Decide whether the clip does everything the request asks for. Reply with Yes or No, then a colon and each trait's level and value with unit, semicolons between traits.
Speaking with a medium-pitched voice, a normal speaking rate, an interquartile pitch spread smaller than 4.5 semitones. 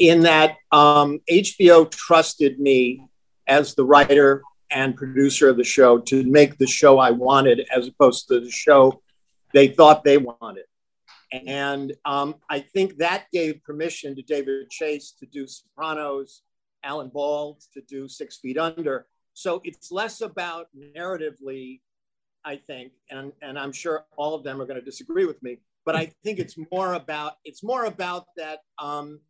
Yes: medium, 145 Hz; average, 165 wpm; average, 3.0 semitones